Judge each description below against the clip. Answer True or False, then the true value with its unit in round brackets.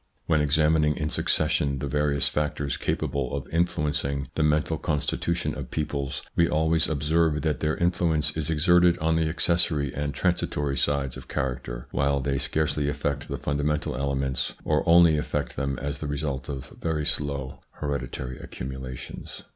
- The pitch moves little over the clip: True (2.2 semitones)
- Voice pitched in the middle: False (75 Hz)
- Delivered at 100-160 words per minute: True (155 wpm)